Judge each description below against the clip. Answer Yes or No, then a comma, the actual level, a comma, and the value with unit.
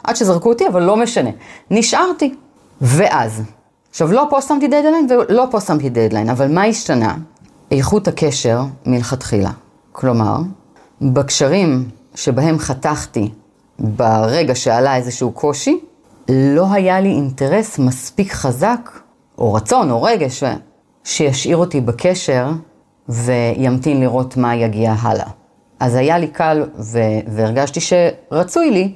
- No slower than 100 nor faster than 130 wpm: Yes, average, 120 wpm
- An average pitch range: No, wide, 7.4 semitones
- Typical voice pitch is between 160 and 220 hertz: No, medium, 140 Hz